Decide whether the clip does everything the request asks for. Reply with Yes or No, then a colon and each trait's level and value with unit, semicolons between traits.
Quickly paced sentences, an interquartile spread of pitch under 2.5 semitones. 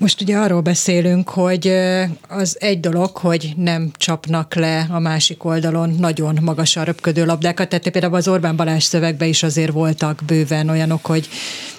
Yes: fast, 160 wpm; narrow, 1.9 semitones